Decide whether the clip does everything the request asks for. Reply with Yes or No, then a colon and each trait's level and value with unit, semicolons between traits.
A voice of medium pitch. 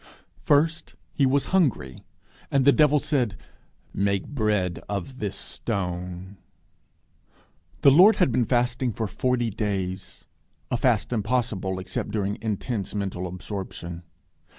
No: low, 110 Hz